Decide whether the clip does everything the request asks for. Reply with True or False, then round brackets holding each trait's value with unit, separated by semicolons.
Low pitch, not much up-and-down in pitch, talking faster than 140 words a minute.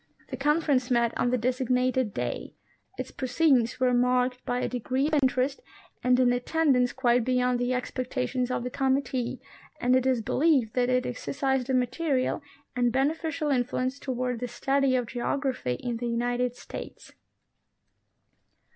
False (255 Hz; 1.4 semitones; 155 wpm)